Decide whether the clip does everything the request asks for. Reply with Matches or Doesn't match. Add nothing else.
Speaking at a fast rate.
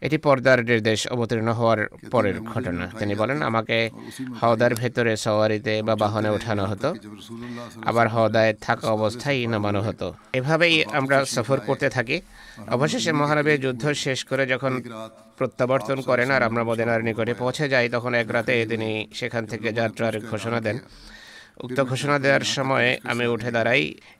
Matches